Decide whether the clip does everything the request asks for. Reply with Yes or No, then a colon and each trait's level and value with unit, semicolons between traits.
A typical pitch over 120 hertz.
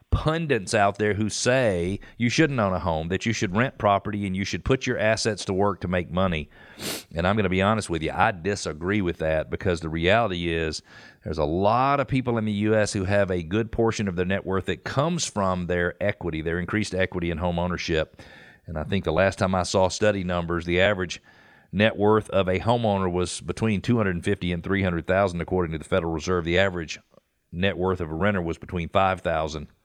No: very low, 95 Hz